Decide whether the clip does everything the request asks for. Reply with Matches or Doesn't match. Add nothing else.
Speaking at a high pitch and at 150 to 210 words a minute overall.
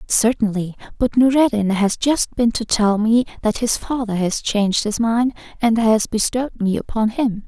Matches